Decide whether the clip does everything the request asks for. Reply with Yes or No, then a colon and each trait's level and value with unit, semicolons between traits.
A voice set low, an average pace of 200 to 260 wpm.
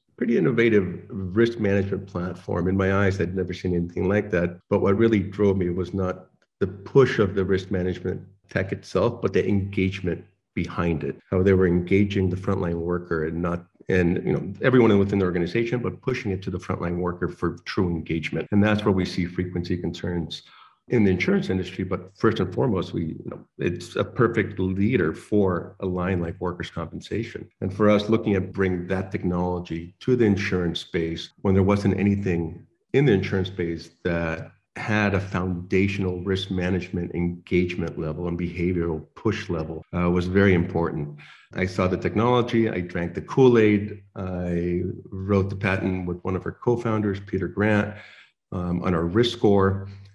No: very low, 95 Hz; average, 175 wpm